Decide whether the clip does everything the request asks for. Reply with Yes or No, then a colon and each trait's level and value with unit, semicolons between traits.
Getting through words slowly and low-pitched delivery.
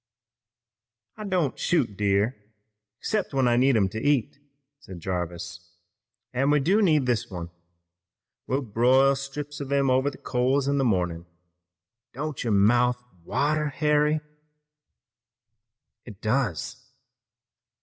Yes: slow, 125 wpm; low, 130 Hz